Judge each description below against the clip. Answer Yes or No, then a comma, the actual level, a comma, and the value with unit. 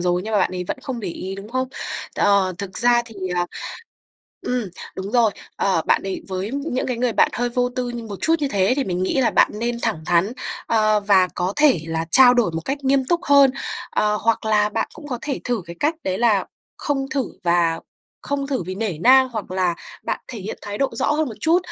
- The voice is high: Yes, high, 225 Hz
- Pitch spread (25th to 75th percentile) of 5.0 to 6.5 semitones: Yes, wide, 5.4 semitones